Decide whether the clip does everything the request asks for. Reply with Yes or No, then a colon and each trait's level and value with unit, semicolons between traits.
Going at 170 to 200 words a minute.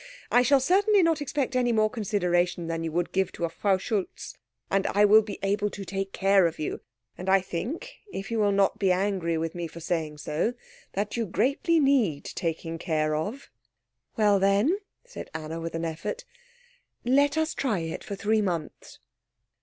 Yes: average, 185 wpm